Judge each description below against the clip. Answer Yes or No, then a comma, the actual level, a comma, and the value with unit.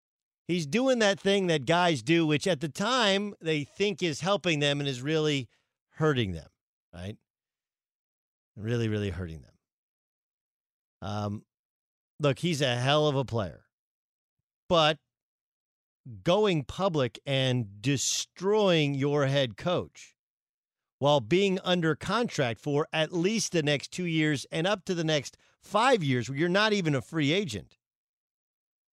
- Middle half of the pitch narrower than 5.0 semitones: No, wide, 5.6 semitones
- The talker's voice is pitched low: No, medium, 150 Hz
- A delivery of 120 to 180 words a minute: Yes, average, 140 wpm